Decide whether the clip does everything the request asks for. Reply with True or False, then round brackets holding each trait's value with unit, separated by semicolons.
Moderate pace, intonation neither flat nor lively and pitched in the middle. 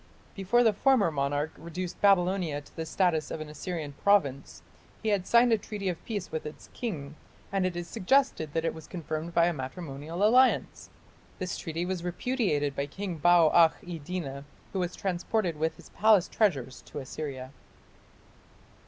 True (170 wpm; 4.3 semitones; 175 Hz)